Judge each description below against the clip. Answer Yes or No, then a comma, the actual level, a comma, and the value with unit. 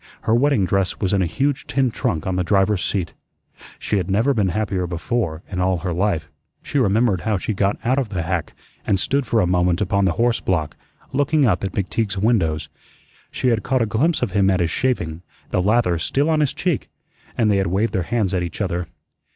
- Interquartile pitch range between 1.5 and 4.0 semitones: No, average, 4.6 semitones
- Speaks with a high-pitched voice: No, low, 100 Hz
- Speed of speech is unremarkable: No, fast, 220 wpm